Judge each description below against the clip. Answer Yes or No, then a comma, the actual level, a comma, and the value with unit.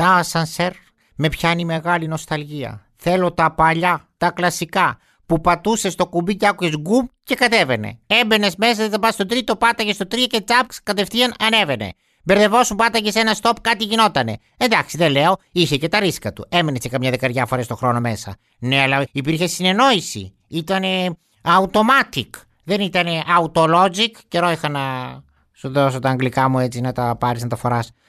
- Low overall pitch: No, medium, 175 Hz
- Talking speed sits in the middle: No, fast, 175 wpm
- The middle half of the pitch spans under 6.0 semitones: No, wide, 7.8 semitones